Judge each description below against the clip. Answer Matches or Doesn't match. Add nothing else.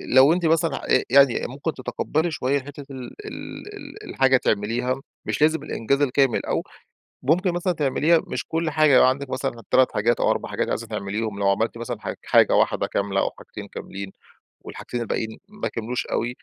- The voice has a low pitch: Matches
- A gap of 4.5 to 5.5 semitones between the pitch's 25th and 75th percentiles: Matches